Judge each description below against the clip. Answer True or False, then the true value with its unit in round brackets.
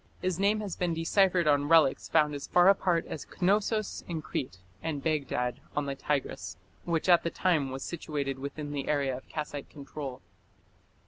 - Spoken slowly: False (175 wpm)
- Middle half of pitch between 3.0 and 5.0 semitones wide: True (4.0 semitones)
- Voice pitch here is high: False (150 Hz)